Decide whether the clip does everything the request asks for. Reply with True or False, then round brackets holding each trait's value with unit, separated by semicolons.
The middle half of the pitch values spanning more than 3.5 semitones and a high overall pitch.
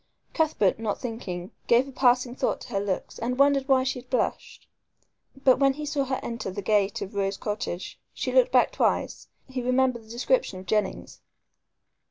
True (4.4 semitones; 245 Hz)